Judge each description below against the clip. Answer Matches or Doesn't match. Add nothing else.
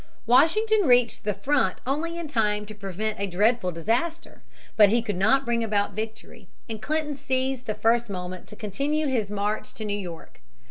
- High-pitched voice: Matches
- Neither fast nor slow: Matches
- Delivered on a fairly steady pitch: Doesn't match